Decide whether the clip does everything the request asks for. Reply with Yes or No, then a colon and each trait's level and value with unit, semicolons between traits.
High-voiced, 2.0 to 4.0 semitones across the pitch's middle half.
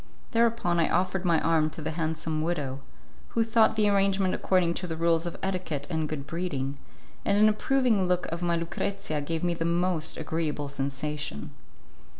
No: medium, 170 Hz; average, 3.2 semitones